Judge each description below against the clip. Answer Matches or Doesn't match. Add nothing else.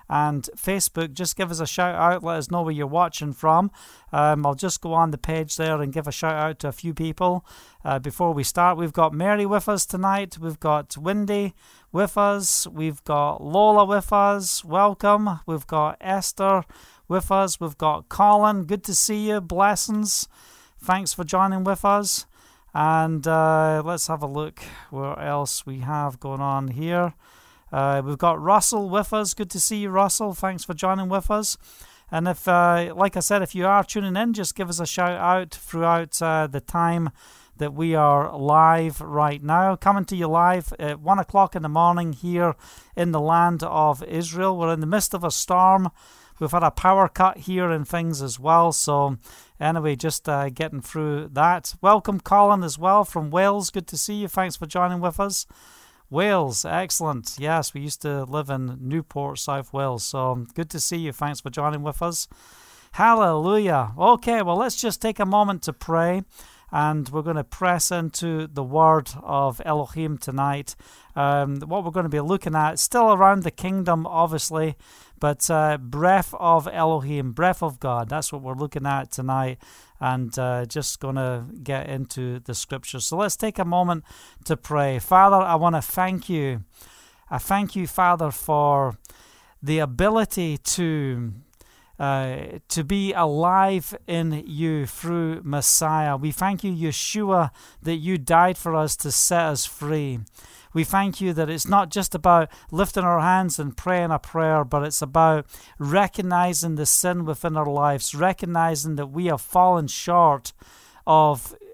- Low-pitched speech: Doesn't match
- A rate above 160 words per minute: Matches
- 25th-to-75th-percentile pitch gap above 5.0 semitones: Doesn't match